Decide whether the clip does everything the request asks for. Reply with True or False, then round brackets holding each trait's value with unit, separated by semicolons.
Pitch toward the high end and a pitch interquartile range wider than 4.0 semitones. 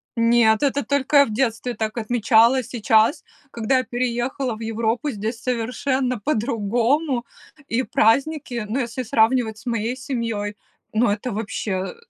False (235 Hz; 2.7 semitones)